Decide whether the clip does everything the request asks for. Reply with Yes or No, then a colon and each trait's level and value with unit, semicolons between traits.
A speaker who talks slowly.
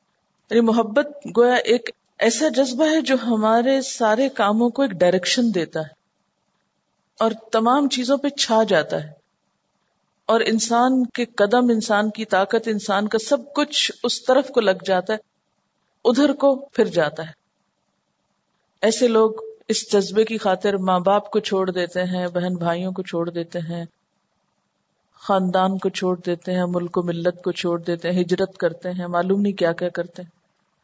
No: average, 160 wpm